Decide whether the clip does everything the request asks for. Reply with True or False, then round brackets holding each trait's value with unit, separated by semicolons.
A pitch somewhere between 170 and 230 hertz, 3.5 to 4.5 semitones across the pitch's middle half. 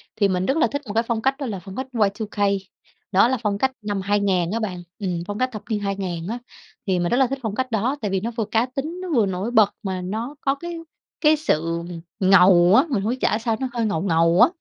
False (210 Hz; 4.9 semitones)